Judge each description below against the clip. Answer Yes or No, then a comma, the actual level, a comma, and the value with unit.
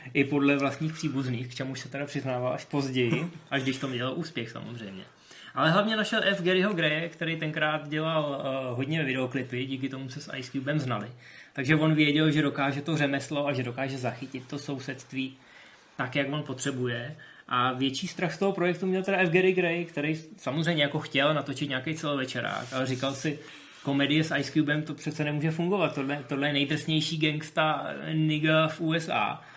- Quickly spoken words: Yes, fast, 185 wpm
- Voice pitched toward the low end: No, medium, 145 Hz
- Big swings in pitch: No, average, 2.8 semitones